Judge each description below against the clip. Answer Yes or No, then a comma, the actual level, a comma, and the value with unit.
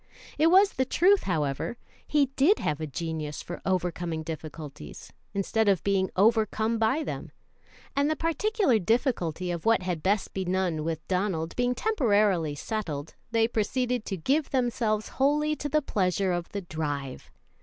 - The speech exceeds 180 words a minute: No, average, 155 wpm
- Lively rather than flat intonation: Yes, wide, 7.3 semitones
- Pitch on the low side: No, high, 200 Hz